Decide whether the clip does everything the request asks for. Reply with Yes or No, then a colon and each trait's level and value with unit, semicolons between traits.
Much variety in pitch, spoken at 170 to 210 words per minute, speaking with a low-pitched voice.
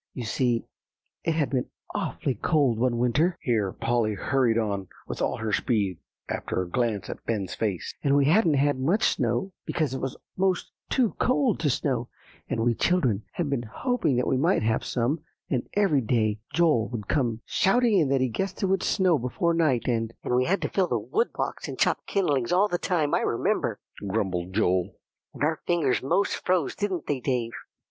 Yes: wide, 6.9 semitones; average, 195 wpm; low, 130 Hz